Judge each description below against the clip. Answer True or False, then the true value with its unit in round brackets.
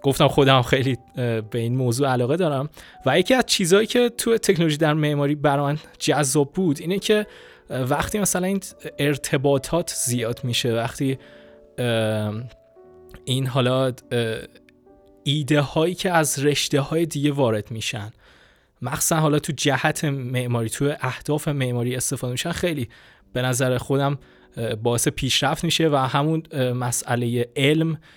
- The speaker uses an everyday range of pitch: True (4.0 semitones)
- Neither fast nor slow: True (130 wpm)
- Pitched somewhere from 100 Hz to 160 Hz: True (140 Hz)